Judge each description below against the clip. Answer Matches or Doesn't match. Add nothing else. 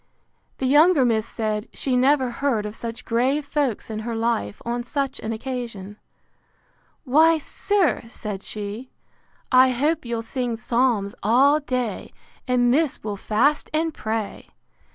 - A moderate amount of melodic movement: Matches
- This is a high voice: Matches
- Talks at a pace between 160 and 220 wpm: Doesn't match